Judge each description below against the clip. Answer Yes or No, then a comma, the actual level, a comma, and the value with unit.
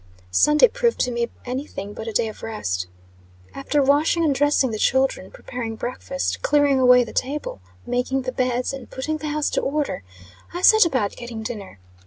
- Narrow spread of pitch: No, average, 3.8 semitones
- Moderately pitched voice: No, very high, 260 Hz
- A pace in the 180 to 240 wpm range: Yes, average, 185 wpm